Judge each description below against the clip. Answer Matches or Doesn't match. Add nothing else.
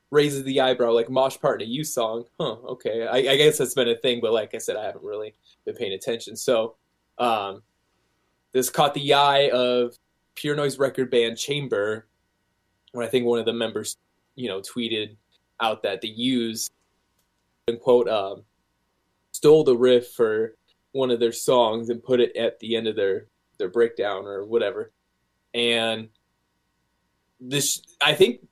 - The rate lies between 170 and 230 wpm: Matches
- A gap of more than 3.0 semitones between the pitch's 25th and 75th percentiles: Matches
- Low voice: Matches